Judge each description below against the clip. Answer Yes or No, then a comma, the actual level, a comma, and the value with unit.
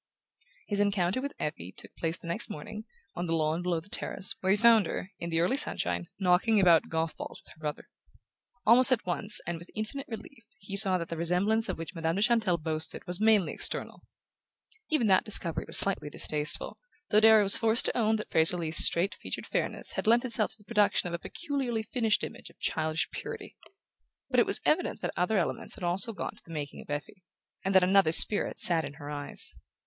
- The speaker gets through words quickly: Yes, fast, 215 wpm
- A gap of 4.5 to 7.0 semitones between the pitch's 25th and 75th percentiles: Yes, average, 4.8 semitones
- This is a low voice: No, medium, 185 Hz